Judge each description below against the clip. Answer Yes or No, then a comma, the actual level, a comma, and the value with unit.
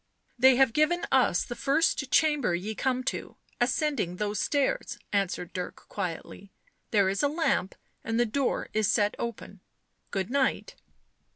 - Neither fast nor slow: Yes, average, 160 wpm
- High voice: Yes, high, 240 Hz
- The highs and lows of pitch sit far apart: Yes, wide, 5.9 semitones